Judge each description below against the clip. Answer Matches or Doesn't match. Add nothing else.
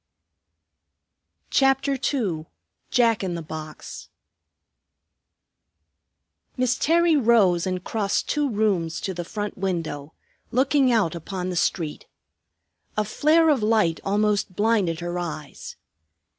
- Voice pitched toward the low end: Doesn't match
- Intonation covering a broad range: Matches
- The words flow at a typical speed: Doesn't match